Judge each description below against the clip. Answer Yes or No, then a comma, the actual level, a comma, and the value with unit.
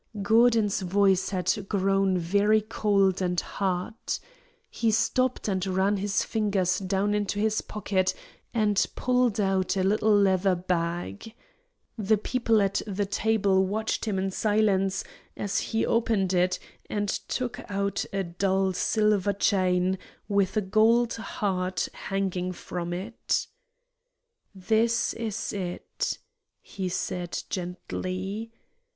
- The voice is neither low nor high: No, high, 195 Hz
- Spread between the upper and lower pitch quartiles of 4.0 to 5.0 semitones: No, narrow, 2.4 semitones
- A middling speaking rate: No, slow, 120 wpm